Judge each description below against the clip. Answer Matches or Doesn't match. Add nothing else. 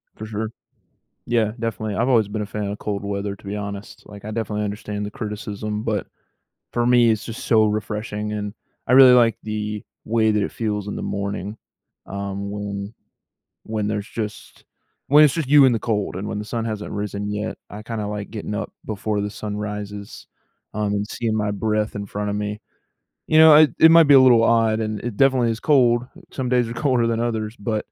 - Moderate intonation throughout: Doesn't match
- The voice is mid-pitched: Doesn't match